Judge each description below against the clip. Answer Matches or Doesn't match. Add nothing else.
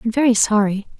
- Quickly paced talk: Doesn't match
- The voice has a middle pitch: Doesn't match